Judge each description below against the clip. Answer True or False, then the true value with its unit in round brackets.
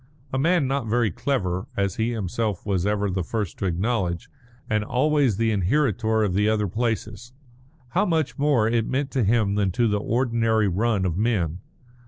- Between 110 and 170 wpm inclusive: False (180 wpm)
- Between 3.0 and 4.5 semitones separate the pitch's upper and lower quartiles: True (3.5 semitones)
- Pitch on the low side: True (110 Hz)